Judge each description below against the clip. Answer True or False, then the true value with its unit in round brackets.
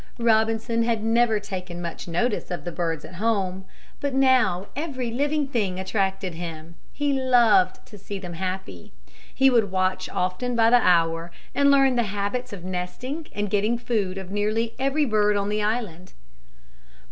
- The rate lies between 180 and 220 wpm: False (165 wpm)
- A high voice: True (210 Hz)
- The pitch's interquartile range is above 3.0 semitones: True (4.7 semitones)